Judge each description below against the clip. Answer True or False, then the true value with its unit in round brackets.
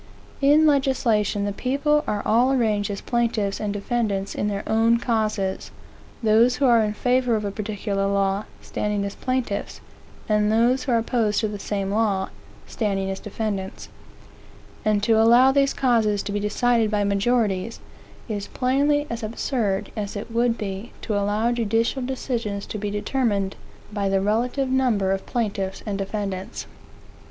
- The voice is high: True (215 Hz)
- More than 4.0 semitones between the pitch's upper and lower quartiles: False (3.1 semitones)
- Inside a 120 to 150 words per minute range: False (160 wpm)